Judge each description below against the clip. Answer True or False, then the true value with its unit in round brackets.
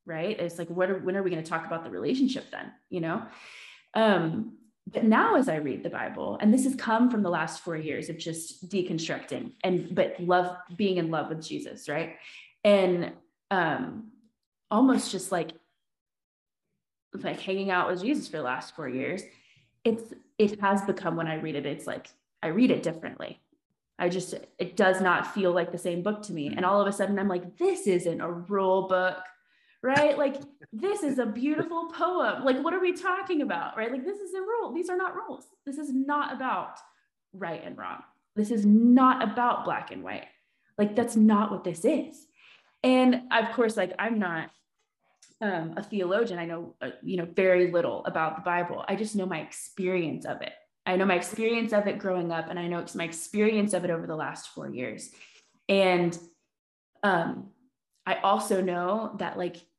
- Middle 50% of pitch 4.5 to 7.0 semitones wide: True (5.6 semitones)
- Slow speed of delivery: False (195 wpm)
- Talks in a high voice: True (195 Hz)